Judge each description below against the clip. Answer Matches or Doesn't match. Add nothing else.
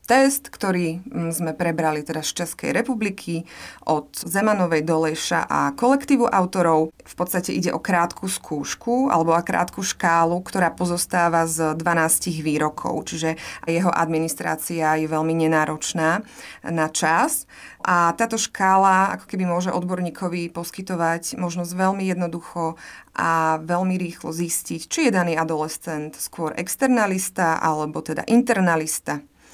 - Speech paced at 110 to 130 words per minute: Matches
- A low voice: Doesn't match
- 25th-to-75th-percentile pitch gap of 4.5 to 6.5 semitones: Doesn't match